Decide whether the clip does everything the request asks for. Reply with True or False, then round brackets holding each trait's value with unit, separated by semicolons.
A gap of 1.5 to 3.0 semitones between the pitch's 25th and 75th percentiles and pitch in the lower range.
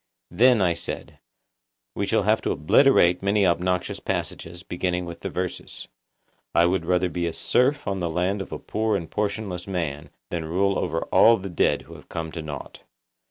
True (2.7 semitones; 90 Hz)